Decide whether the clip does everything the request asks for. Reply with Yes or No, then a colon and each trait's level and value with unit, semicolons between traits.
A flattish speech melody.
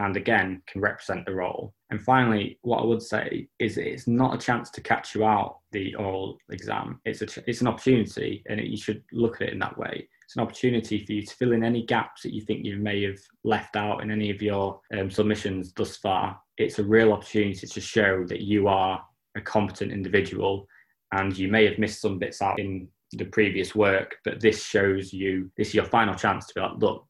Yes: narrow, 2.1 semitones